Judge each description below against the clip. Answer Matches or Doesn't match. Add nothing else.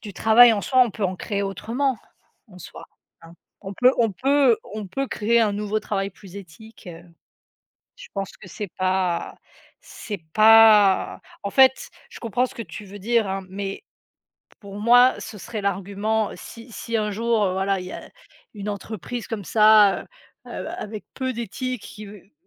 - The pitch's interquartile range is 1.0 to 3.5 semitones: Matches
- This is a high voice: Matches